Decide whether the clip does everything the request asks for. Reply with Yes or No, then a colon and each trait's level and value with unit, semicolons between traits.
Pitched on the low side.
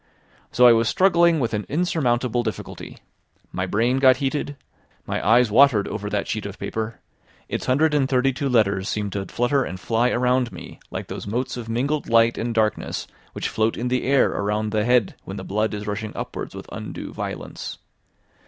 Yes: low, 120 Hz